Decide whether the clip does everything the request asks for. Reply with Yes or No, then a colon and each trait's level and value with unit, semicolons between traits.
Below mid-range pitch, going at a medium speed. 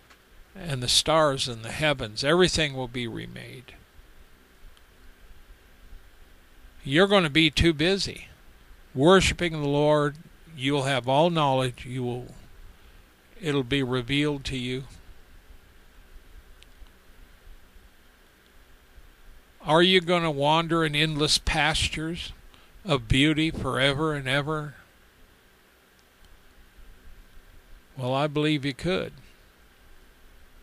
No: low, 120 Hz; slow, 95 wpm